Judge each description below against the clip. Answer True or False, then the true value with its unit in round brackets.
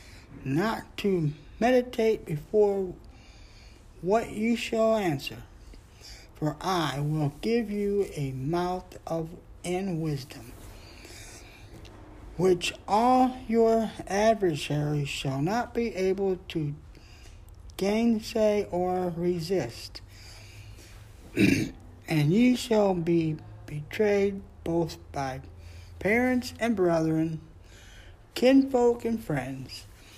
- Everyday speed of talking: False (85 wpm)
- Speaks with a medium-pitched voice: True (160 Hz)